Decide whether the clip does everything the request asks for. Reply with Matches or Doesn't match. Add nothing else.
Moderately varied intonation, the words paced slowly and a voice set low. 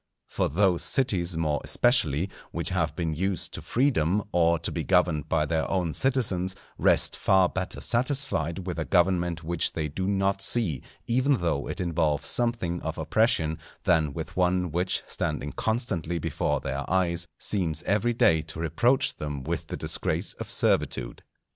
Doesn't match